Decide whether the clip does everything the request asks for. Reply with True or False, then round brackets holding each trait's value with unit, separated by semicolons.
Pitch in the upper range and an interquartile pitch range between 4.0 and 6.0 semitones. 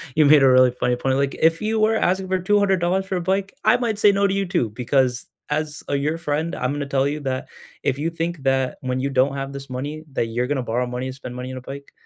False (140 Hz; 5.5 semitones)